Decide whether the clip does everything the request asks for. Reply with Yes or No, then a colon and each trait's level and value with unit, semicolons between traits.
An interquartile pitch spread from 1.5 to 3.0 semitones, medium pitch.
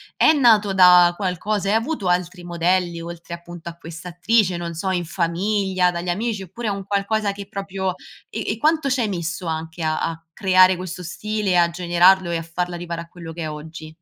Yes: average, 2.7 semitones; medium, 180 Hz